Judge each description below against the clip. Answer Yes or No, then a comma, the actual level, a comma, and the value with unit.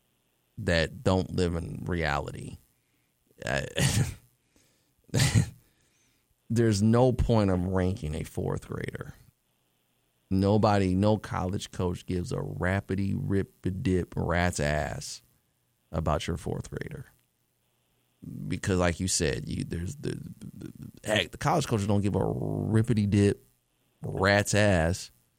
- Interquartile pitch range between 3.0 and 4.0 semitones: Yes, average, 3.3 semitones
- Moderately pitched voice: No, very low, 95 Hz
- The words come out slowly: Yes, slow, 120 wpm